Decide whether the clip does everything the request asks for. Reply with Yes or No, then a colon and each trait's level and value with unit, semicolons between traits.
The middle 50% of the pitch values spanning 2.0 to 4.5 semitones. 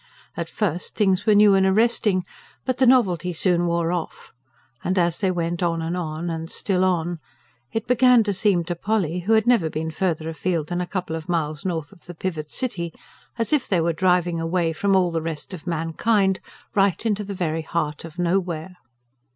Yes: average, 2.9 semitones